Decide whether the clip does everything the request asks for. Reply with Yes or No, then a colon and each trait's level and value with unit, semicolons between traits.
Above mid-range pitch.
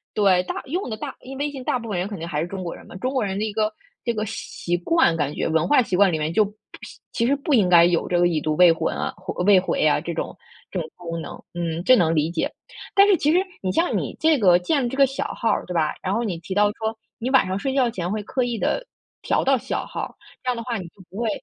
Yes: high, 200 Hz